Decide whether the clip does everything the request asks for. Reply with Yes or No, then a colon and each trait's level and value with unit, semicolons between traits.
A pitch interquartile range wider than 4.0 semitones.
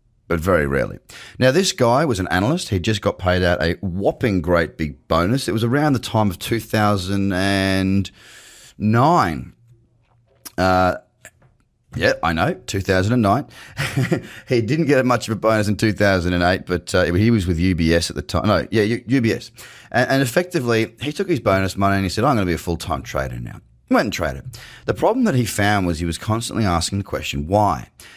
Yes: average, 4.8 semitones